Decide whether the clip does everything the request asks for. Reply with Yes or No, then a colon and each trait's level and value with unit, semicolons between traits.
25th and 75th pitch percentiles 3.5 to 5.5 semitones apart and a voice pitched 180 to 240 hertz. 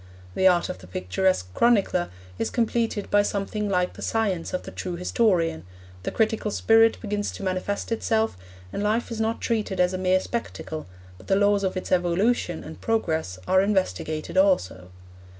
Yes: average, 3.9 semitones; high, 190 Hz